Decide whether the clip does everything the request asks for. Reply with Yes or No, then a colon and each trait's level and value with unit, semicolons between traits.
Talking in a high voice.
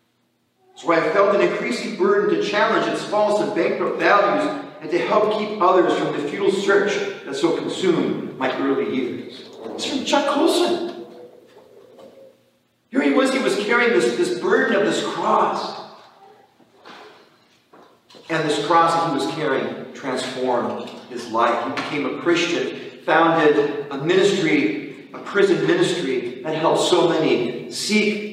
Yes: high, 210 Hz